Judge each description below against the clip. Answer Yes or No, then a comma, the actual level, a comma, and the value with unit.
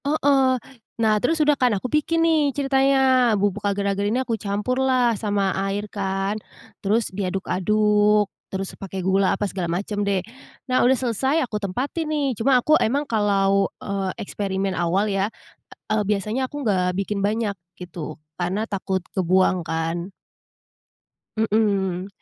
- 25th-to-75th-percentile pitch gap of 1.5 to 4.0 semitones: No, average, 4.6 semitones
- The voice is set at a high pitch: Yes, high, 205 Hz